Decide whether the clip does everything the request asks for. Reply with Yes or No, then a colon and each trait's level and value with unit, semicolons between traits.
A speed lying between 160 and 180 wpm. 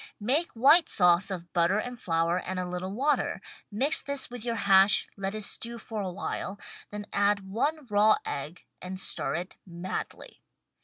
Yes: average, 170 wpm